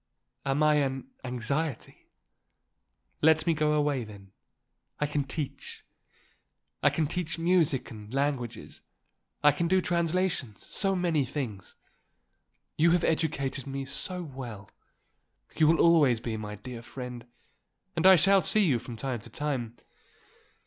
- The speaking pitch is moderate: Yes, medium, 145 Hz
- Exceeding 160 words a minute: No, slow, 135 wpm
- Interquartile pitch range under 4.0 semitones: No, average, 4.9 semitones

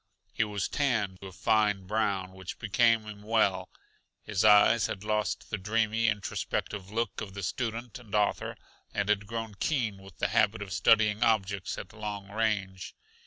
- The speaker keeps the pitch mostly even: Yes, narrow, 2.2 semitones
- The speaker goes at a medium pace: Yes, average, 165 wpm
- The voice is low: Yes, low, 105 Hz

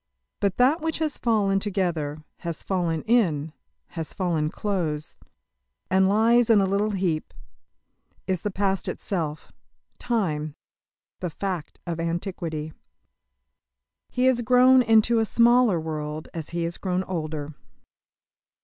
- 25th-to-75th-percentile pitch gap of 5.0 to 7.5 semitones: Yes, wide, 5.5 semitones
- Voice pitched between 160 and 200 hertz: Yes, medium, 185 Hz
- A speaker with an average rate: No, slow, 125 wpm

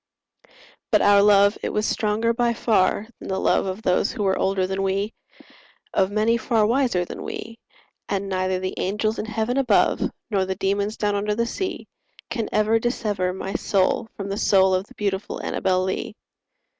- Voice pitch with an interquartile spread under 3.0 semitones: Yes, narrow, 2.5 semitones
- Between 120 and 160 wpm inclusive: No, average, 180 wpm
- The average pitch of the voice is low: No, high, 205 Hz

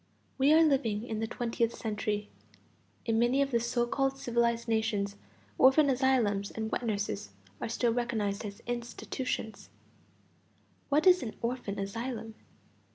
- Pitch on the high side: Yes, high, 235 Hz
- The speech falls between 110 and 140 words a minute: Yes, slow, 135 wpm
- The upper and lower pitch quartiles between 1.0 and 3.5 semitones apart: Yes, average, 2.9 semitones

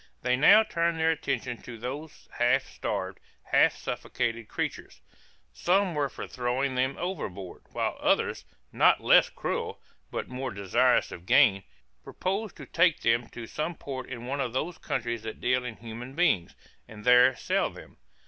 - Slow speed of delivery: No, average, 160 wpm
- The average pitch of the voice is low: Yes, low, 125 Hz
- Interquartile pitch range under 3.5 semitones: No, average, 4.8 semitones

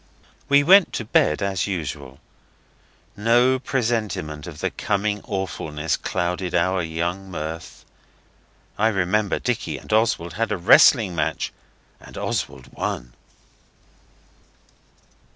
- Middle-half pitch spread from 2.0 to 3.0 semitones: No, average, 4.9 semitones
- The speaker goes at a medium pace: No, slow, 110 wpm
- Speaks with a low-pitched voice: Yes, very low, 95 Hz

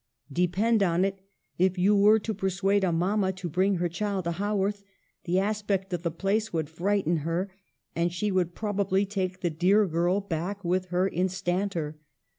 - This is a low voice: No, high, 190 Hz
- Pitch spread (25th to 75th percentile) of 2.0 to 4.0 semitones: Yes, narrow, 2.4 semitones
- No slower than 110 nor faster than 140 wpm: No, average, 180 wpm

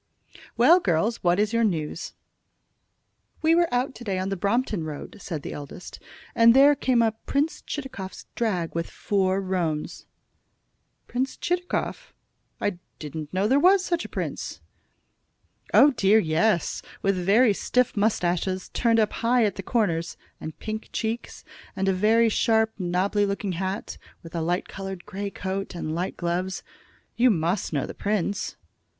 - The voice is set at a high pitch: Yes, high, 200 Hz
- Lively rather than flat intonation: No, average, 4.6 semitones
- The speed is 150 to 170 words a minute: Yes, average, 155 wpm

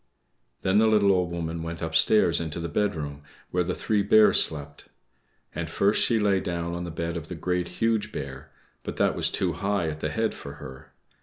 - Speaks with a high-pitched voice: No, very low, 85 Hz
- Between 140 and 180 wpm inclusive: No, fast, 205 wpm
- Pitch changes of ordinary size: Yes, average, 3.7 semitones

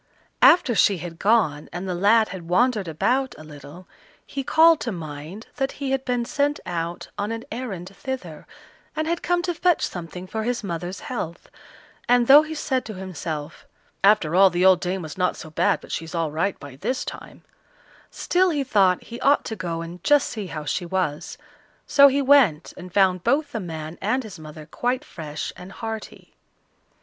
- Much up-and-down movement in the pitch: Yes, wide, 7.2 semitones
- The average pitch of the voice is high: Yes, high, 195 Hz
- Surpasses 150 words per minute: Yes, average, 190 wpm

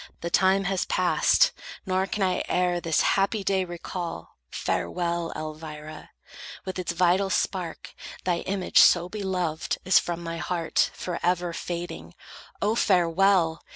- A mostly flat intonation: Yes, narrow, 2.1 semitones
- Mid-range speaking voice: Yes, medium, 180 Hz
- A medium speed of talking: No, slow, 130 wpm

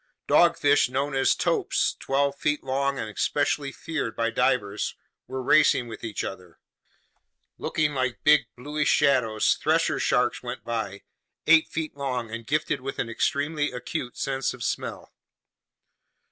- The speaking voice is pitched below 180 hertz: Yes, low, 135 Hz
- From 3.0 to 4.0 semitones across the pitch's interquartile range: Yes, average, 3.5 semitones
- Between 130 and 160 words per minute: Yes, average, 140 wpm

